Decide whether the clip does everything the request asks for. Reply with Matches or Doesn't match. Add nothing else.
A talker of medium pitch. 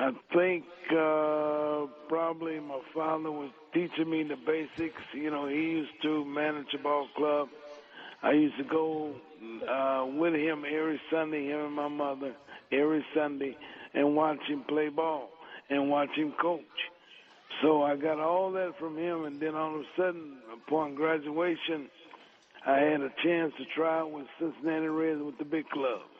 Matches